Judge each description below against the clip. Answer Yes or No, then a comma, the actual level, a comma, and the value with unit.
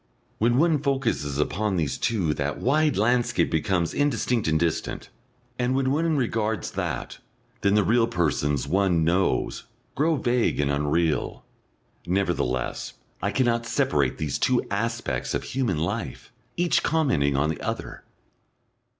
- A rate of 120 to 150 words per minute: Yes, slow, 135 wpm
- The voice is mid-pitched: No, low, 105 Hz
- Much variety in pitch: Yes, wide, 8.2 semitones